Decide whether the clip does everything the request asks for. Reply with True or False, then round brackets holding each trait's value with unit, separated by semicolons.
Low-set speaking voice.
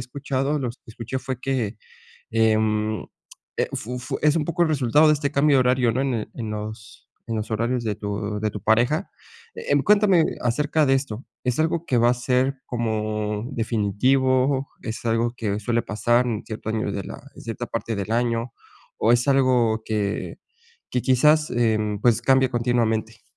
True (120 Hz)